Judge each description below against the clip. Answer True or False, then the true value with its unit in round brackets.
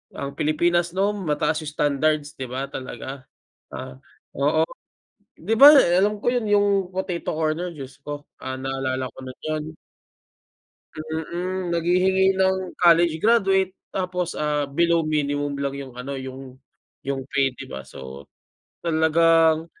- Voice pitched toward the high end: False (155 Hz)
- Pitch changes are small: False (4.5 semitones)